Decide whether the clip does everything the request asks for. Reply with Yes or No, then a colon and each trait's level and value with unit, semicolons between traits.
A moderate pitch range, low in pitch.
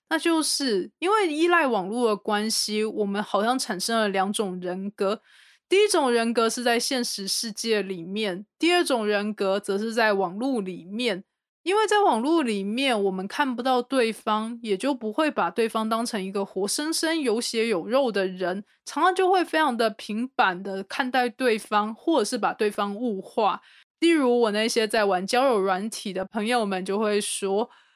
No: average, 4.4 semitones; high, 225 Hz